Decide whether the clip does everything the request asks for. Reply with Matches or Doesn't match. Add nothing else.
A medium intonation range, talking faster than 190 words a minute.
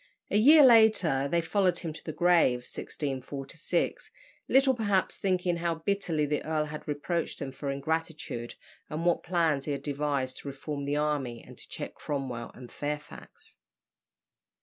Doesn't match